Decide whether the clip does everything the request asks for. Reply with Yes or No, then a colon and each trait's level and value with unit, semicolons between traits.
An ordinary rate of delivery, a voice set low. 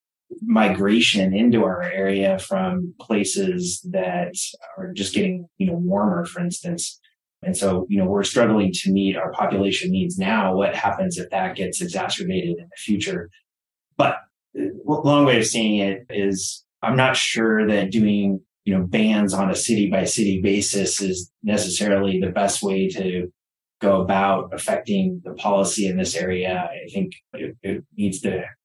Yes: average, 165 wpm; low, 105 Hz